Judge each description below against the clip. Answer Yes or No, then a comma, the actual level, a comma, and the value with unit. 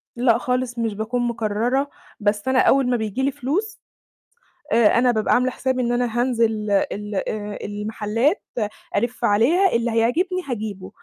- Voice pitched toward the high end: Yes, high, 235 Hz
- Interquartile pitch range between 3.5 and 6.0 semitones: No, average, 3.1 semitones